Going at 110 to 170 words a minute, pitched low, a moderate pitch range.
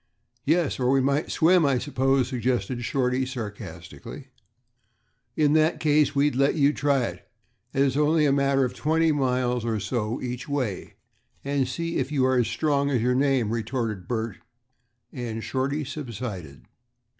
Yes: average, 155 wpm; low, 130 Hz; average, 3.0 semitones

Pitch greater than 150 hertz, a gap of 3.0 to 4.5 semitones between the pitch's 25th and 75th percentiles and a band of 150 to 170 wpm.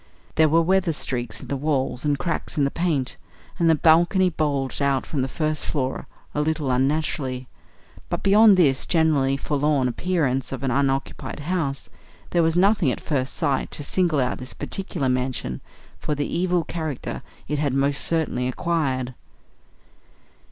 No: medium, 145 Hz; average, 3.7 semitones; average, 160 wpm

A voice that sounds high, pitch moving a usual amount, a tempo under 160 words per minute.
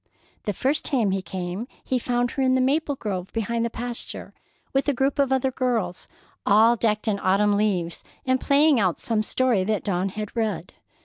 No: high, 230 Hz; average, 4.4 semitones; average, 190 wpm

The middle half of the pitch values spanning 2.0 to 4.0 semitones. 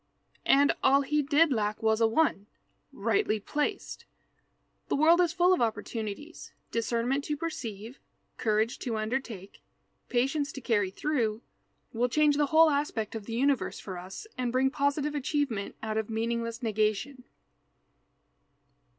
No: average, 4.9 semitones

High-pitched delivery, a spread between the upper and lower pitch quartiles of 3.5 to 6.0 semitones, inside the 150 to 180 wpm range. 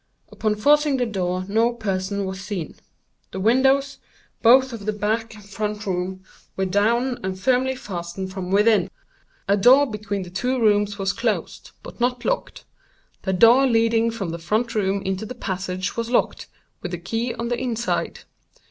Yes: high, 210 Hz; average, 3.9 semitones; average, 170 wpm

